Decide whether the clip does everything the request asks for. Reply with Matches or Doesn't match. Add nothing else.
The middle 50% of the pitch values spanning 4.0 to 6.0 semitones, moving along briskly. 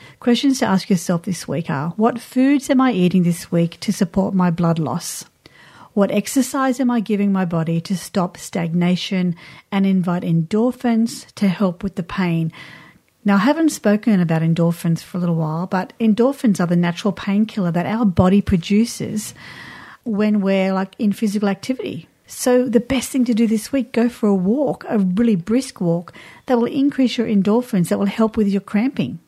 Doesn't match